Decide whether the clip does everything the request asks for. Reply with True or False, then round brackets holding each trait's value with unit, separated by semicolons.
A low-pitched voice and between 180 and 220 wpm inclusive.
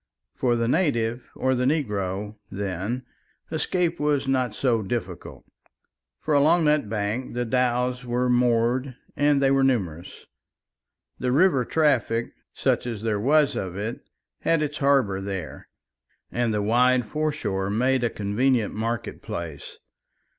False (125 Hz; 135 wpm)